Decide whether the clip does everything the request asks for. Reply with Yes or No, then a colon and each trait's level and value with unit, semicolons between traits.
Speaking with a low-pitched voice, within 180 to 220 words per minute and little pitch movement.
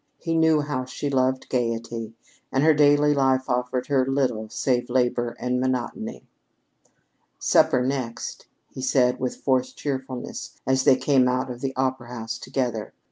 No: low, 130 Hz; average, 150 wpm; narrow, 1.5 semitones